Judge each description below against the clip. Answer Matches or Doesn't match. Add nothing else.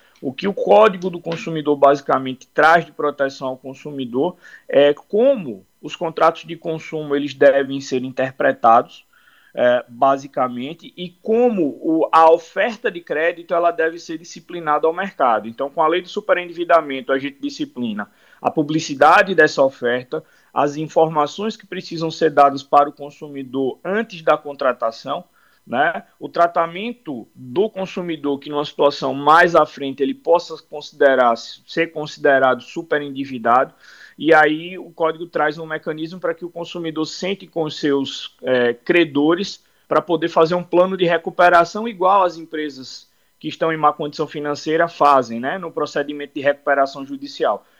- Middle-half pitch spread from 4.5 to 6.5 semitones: Doesn't match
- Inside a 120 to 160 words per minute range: Matches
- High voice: Doesn't match